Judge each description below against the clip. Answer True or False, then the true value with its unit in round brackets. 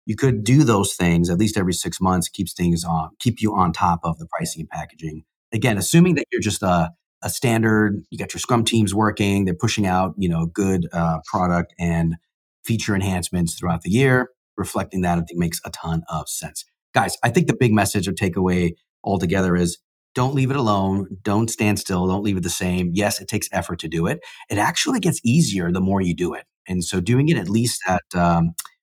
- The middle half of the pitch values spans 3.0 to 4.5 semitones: True (3.9 semitones)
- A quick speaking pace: True (220 wpm)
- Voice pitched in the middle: False (95 Hz)